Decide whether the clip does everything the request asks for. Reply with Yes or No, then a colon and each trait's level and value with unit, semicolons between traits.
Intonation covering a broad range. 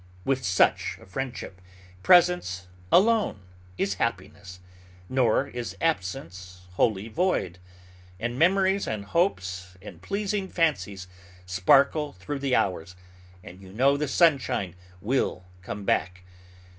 Yes: wide, 8.2 semitones